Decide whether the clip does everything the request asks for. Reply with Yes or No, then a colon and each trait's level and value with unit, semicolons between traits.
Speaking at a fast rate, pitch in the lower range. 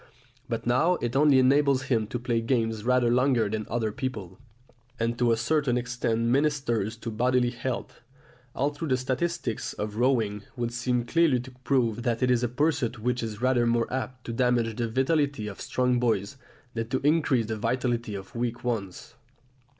No: average, 175 wpm; low, 120 Hz